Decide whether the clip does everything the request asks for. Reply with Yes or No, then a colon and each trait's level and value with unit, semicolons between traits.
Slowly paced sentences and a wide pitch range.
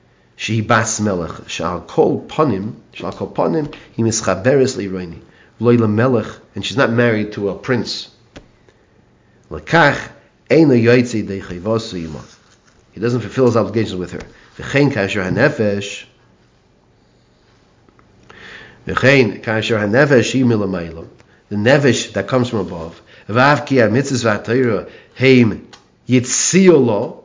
No: slow, 130 wpm; average, 4.2 semitones